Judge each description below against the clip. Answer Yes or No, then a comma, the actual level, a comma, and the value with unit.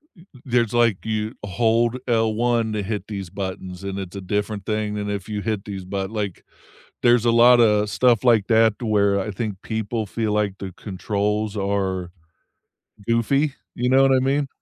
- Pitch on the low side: Yes, low, 105 Hz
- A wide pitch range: No, average, 2.7 semitones